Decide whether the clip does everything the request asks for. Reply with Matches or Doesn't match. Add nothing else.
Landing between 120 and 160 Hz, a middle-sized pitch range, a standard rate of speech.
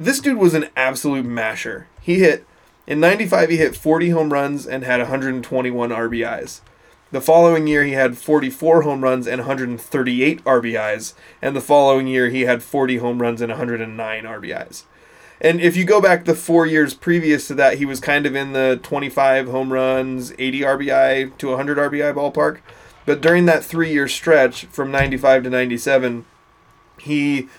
Matches